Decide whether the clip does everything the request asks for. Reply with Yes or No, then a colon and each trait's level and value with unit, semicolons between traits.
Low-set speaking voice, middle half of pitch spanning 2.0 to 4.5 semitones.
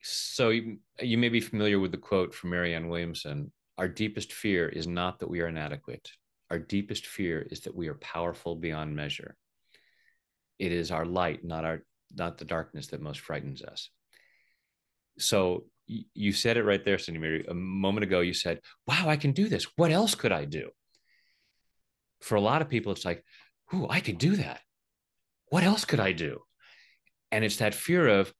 No: very low, 95 Hz; average, 5.1 semitones